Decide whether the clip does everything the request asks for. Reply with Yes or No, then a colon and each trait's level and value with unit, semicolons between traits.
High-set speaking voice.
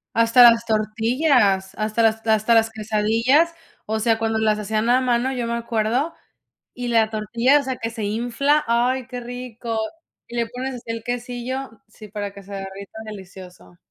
Yes: high, 230 Hz